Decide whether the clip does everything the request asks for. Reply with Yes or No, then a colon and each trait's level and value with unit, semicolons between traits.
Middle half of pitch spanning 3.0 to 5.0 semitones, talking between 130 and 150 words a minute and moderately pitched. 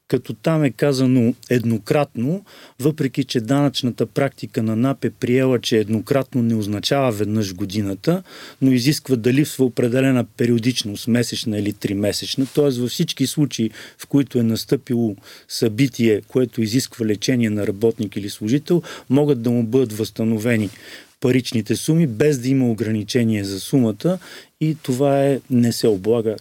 No: average, 3.7 semitones; average, 145 wpm; low, 125 Hz